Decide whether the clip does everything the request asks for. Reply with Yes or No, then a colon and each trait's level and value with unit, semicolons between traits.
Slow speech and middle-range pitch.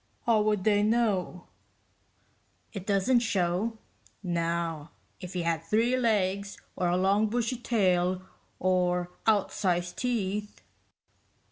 No: slow, 110 wpm; high, 195 Hz